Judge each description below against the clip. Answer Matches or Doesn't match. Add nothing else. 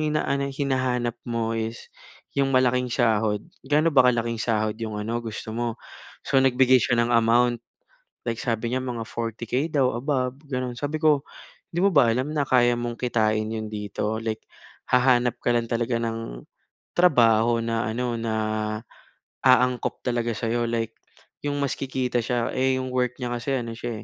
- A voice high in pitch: Doesn't match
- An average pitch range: Doesn't match